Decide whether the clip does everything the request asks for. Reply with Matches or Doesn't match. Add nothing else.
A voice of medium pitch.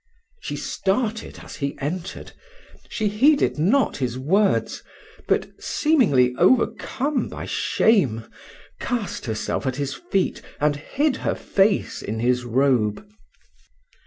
Matches